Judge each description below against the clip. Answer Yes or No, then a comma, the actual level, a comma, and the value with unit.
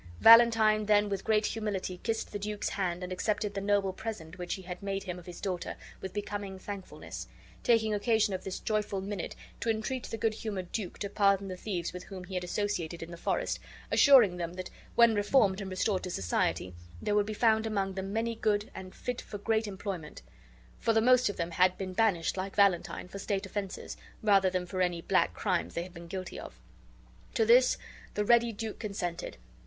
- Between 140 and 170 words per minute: No, fast, 205 wpm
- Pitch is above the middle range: Yes, high, 200 Hz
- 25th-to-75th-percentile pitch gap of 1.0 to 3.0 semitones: Yes, average, 2.7 semitones